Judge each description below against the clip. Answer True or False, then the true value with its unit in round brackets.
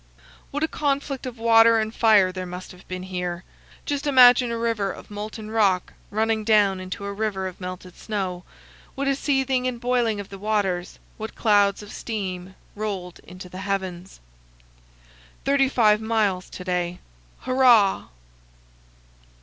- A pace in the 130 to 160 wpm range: True (150 wpm)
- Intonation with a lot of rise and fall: False (3.9 semitones)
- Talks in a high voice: True (210 Hz)